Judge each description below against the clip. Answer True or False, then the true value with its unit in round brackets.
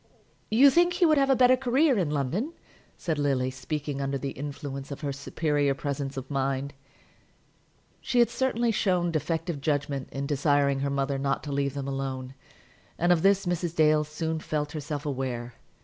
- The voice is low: False (145 Hz)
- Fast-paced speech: False (175 wpm)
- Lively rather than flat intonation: False (4.3 semitones)